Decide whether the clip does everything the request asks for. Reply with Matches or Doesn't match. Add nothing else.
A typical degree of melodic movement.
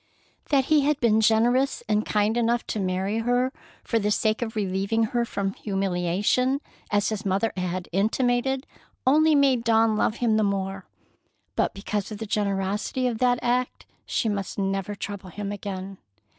Matches